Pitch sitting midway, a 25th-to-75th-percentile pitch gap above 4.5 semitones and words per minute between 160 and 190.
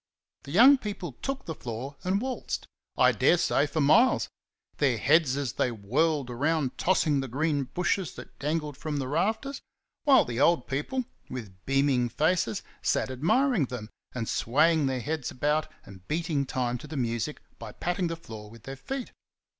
Yes: medium, 145 Hz; average, 5.1 semitones; average, 170 wpm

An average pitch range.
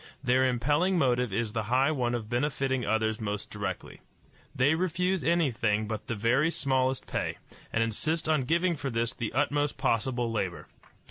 Yes: average, 4.5 semitones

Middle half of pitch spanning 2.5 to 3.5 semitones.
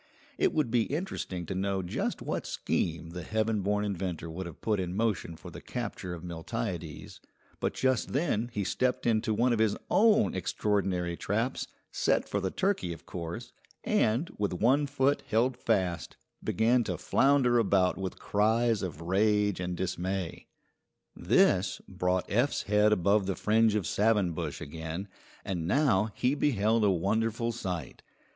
No: average, 4.2 semitones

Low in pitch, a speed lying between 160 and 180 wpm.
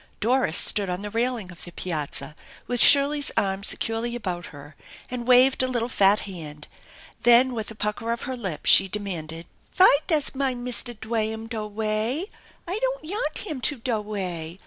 No: high, 225 Hz; average, 175 wpm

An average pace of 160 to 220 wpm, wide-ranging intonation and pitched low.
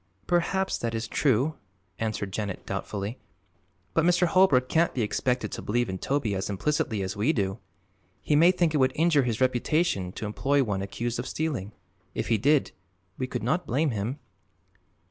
Yes: average, 175 wpm; wide, 6.5 semitones; low, 125 Hz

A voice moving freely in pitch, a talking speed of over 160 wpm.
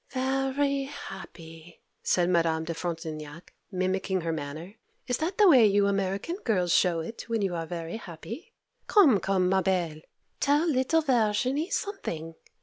No: wide, 7.9 semitones; average, 145 wpm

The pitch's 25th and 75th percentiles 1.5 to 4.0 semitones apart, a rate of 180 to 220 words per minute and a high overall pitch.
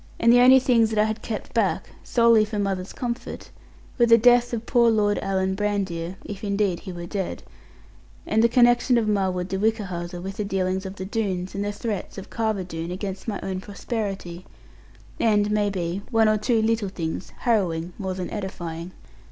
Yes: average, 3.1 semitones; average, 190 wpm; high, 205 Hz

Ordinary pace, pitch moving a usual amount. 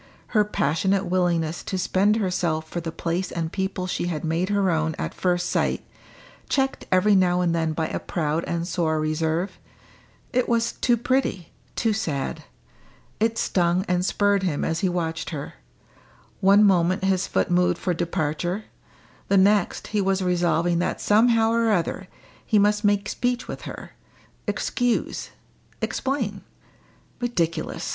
Yes: average, 150 wpm; average, 3.5 semitones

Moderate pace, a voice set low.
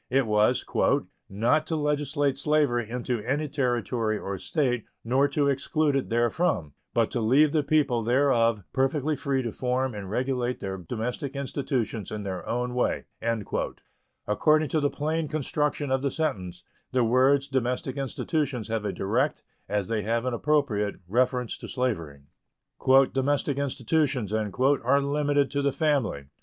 Yes: average, 150 wpm; low, 130 Hz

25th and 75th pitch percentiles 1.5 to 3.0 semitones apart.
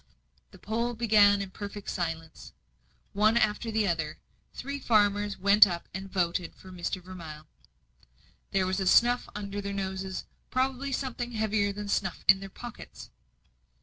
Yes: average, 2.7 semitones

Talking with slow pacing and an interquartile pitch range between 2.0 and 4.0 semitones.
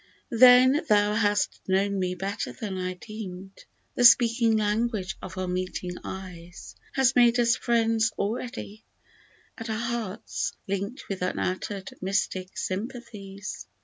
Yes: slow, 130 wpm; average, 3.6 semitones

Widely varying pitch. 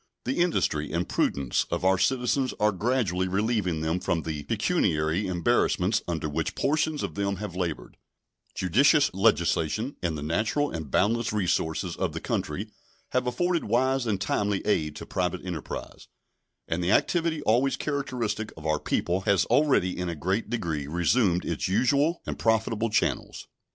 Yes: wide, 6.2 semitones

